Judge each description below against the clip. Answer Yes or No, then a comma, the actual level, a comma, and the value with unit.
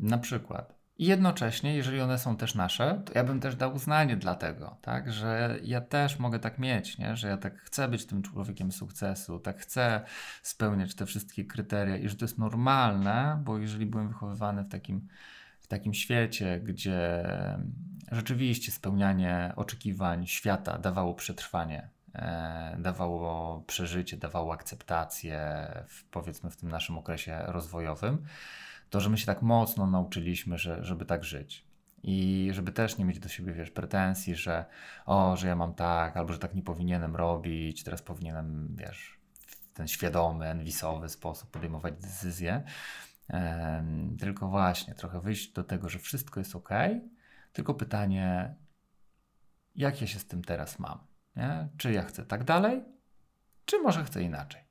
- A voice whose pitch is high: No, very low, 95 Hz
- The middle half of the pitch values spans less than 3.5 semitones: No, average, 5.0 semitones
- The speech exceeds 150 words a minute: Yes, fast, 160 wpm